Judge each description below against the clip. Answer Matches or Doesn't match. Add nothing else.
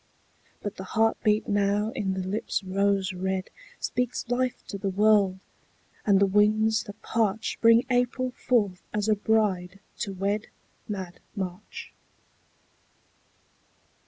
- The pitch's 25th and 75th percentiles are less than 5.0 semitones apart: Matches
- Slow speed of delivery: Matches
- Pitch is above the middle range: Matches